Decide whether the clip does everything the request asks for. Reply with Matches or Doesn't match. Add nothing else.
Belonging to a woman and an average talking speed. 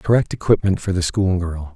Doesn't match